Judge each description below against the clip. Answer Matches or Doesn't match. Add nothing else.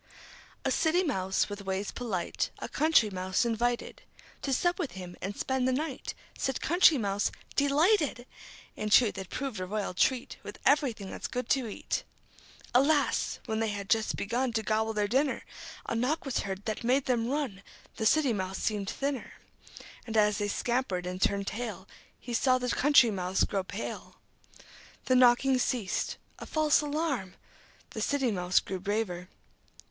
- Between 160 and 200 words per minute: Matches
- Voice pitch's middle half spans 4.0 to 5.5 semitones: Matches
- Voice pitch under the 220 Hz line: Doesn't match